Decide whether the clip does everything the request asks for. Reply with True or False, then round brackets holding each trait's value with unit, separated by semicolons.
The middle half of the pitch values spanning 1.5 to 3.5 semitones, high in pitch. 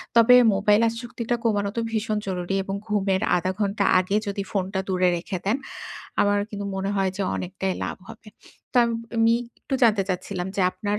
True (2.5 semitones; 200 Hz)